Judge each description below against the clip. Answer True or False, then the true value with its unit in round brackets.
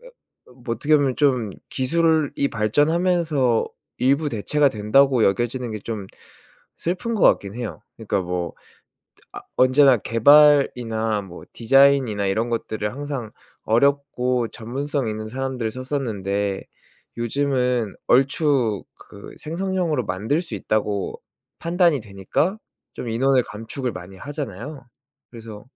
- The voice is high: False (125 Hz)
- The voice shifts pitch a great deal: False (4.8 semitones)